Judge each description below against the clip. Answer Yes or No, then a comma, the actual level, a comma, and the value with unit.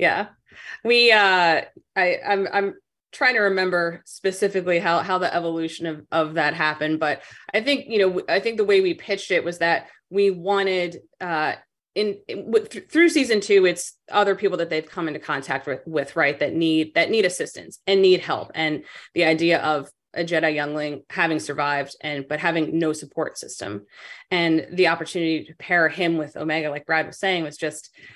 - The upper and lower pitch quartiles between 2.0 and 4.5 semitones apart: Yes, average, 4.0 semitones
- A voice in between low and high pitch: Yes, medium, 170 Hz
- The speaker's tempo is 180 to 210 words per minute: Yes, average, 190 wpm